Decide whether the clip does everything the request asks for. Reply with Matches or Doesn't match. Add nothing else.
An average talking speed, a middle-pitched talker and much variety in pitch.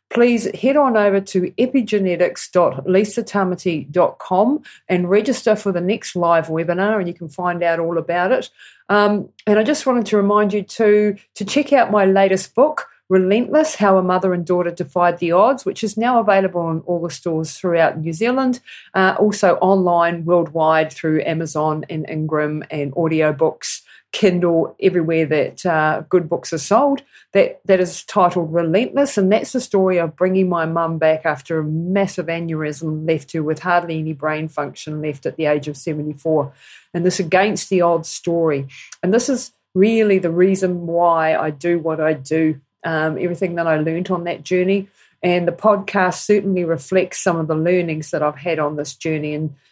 Doesn't match